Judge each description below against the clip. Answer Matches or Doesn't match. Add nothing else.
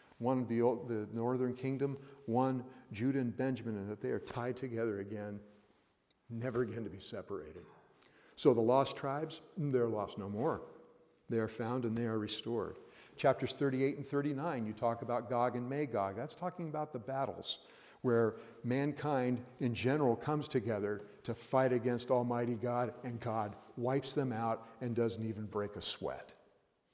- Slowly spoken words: Doesn't match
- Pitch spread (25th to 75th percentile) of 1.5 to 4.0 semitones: Matches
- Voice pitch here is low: Matches